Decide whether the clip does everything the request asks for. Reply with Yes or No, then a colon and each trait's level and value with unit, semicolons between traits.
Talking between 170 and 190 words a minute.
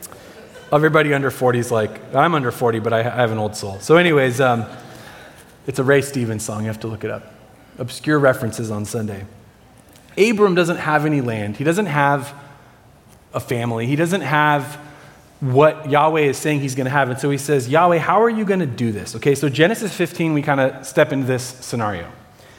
No: average, 200 wpm